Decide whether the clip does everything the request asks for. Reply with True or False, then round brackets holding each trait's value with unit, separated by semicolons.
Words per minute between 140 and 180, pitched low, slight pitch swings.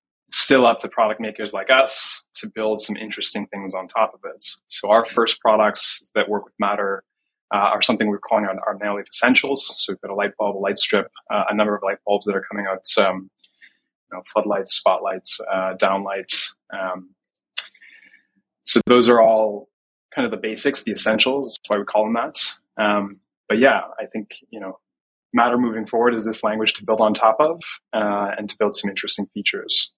False (200 wpm; 105 Hz; 2.0 semitones)